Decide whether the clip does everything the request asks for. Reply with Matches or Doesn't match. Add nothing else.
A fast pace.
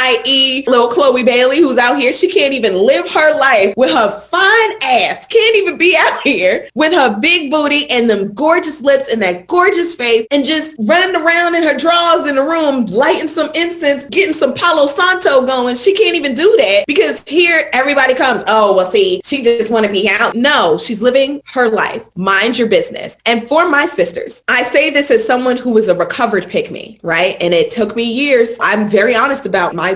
Matches